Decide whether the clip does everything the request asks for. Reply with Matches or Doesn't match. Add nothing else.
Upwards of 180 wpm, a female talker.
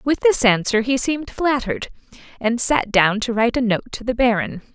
Matches